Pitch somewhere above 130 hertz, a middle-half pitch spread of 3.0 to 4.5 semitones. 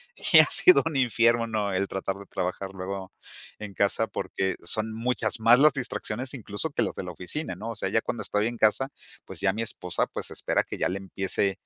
No: low, 105 Hz; average, 3.4 semitones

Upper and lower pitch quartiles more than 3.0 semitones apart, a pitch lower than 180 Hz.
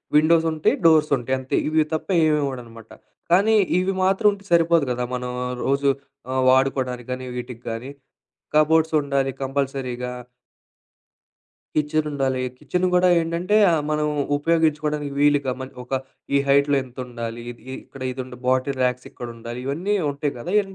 Yes: average, 3.8 semitones; medium, 140 Hz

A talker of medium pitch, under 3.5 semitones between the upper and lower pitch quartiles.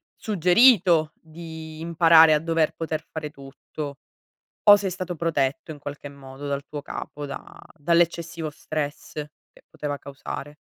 Yes: medium, 155 Hz; narrow, 2.5 semitones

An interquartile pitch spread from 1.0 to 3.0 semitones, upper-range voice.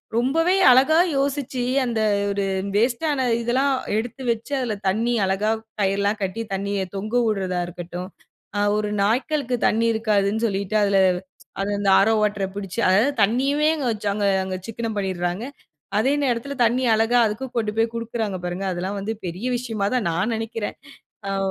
No: average, 3.7 semitones; high, 220 Hz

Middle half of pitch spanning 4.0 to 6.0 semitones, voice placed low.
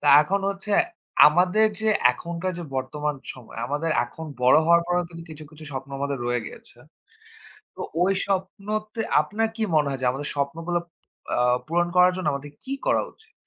No: average, 4.7 semitones; medium, 165 Hz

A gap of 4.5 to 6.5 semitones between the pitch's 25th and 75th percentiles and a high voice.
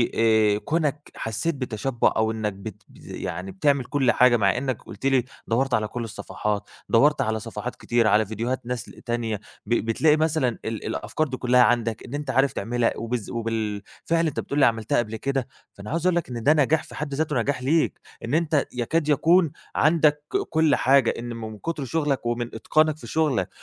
No: average, 4.8 semitones; low, 125 Hz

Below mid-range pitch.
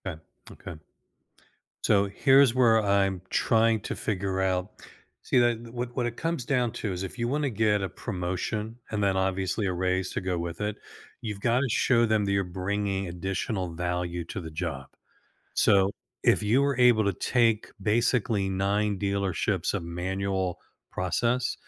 Yes: low, 100 Hz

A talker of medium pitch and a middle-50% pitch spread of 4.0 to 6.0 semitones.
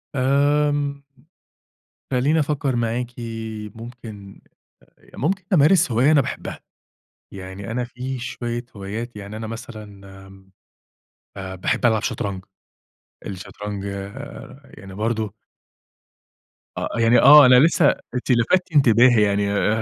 No: low, 120 Hz; average, 5.0 semitones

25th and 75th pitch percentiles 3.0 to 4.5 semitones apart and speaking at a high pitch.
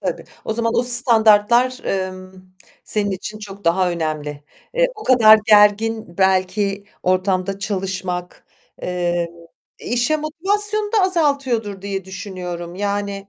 Yes: average, 4.1 semitones; high, 200 Hz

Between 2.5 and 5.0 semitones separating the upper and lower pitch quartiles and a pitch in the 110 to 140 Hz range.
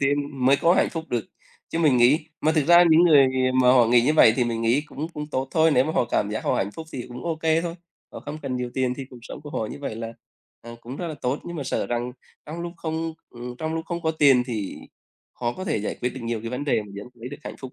Yes: average, 4.5 semitones; low, 135 Hz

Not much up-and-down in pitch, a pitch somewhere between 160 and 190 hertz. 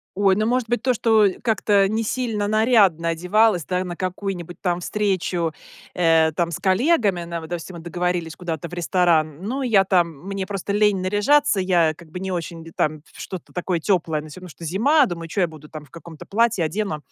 No: average, 3.7 semitones; medium, 185 Hz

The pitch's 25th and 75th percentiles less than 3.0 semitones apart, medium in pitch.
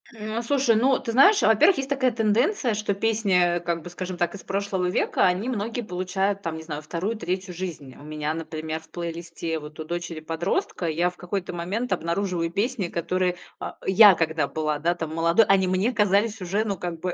No: average, 4.2 semitones; medium, 180 Hz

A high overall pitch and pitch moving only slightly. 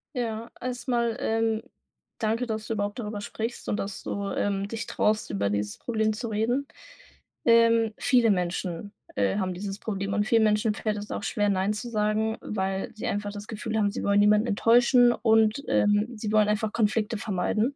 Yes: high, 215 Hz; narrow, 1.9 semitones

